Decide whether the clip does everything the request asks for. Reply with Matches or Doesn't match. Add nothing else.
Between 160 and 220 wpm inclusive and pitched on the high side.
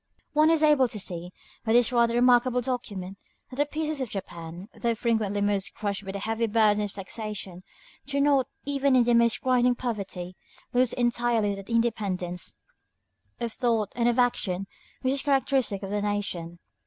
Matches